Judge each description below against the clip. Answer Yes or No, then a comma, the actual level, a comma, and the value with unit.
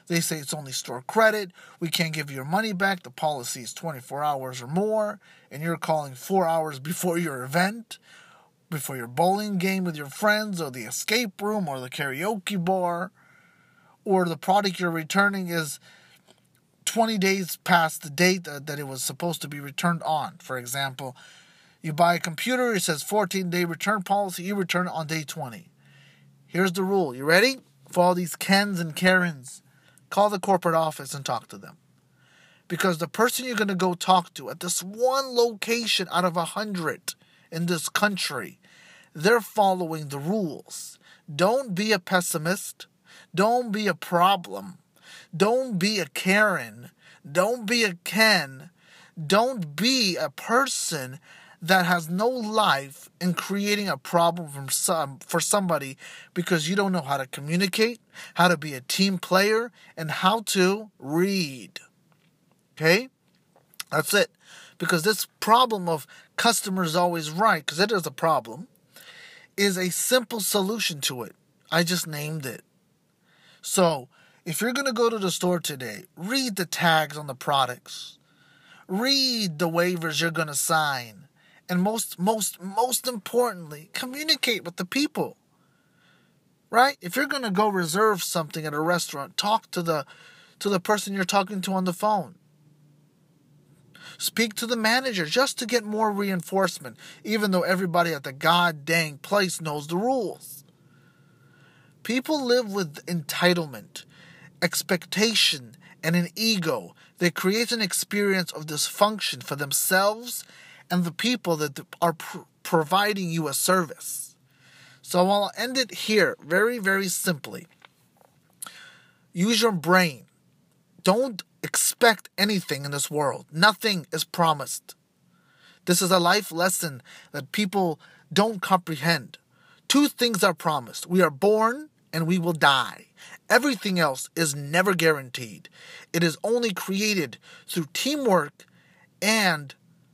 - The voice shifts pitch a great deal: No, average, 4.4 semitones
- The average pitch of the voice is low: No, medium, 180 Hz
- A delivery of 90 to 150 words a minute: Yes, average, 145 wpm